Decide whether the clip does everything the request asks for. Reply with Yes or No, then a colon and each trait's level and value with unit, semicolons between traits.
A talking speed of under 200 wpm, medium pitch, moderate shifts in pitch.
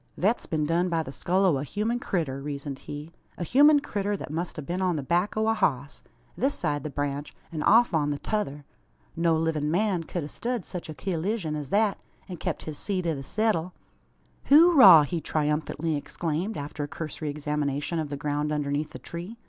No: fast, 205 wpm; medium, 160 Hz; average, 4.8 semitones